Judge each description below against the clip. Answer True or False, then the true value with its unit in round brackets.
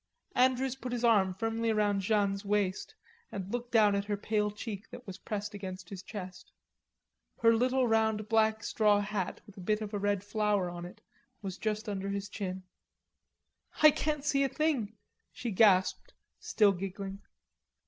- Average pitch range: False (2.3 semitones)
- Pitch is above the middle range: True (210 Hz)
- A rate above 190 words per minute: False (170 wpm)